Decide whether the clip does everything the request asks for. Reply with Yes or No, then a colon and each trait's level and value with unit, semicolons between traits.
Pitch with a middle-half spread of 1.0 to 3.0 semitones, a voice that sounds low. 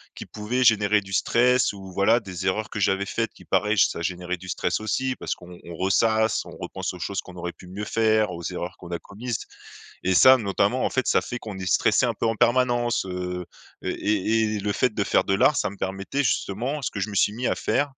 No: average, 3.6 semitones; low, 105 Hz